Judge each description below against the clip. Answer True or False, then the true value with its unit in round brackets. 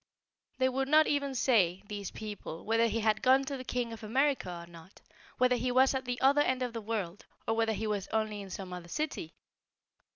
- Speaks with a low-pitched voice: False (225 Hz)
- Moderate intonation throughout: True (4.3 semitones)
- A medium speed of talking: False (220 wpm)